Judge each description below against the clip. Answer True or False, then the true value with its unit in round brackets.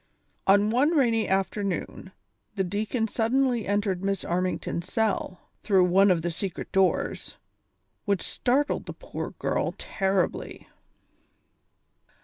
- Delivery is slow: True (115 wpm)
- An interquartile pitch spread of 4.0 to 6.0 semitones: False (3.1 semitones)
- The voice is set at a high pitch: True (200 Hz)